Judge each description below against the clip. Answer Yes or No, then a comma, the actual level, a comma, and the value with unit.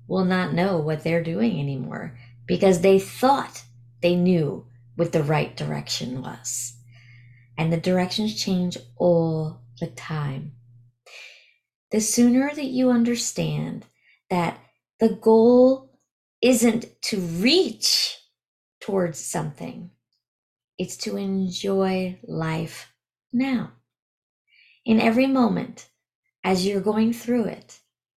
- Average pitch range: No, wide, 8.7 semitones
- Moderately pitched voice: Yes, medium, 180 Hz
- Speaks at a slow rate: Yes, slow, 105 wpm